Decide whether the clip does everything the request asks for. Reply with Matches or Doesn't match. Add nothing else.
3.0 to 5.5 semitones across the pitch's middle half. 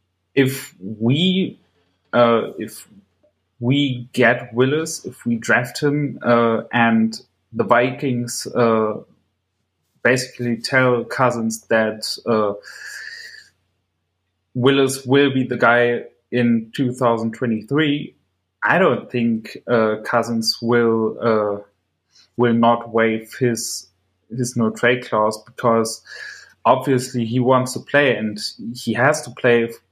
Doesn't match